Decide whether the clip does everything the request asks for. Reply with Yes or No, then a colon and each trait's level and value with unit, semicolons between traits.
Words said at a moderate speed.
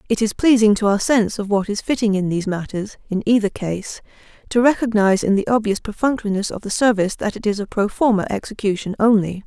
No: fast, 210 wpm